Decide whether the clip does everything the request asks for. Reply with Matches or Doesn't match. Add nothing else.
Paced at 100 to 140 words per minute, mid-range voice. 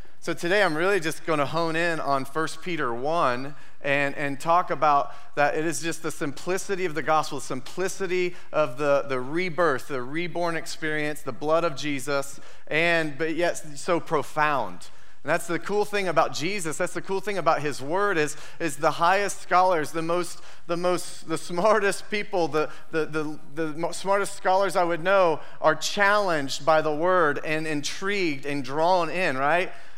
Doesn't match